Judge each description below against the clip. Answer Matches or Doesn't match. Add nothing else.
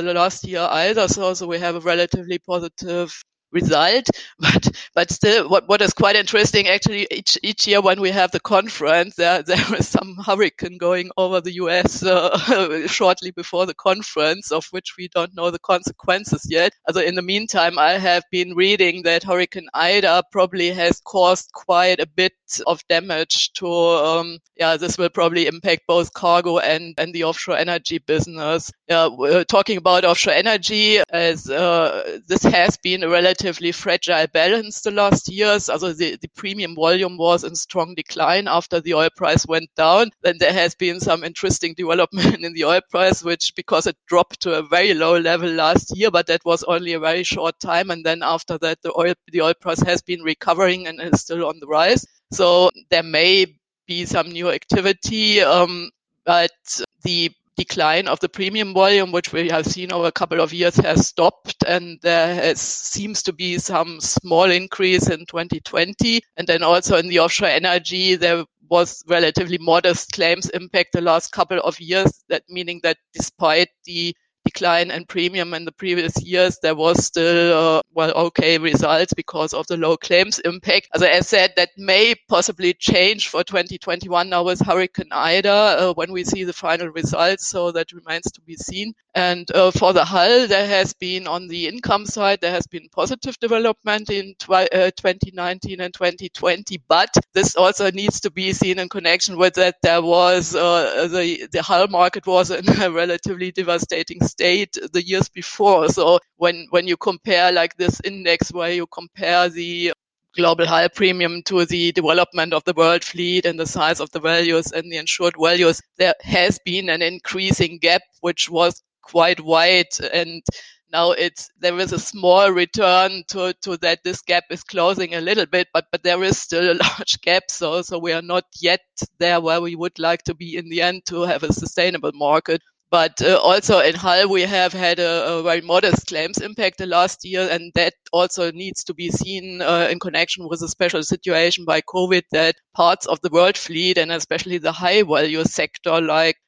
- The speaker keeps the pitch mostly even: Matches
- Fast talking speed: Doesn't match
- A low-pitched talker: Doesn't match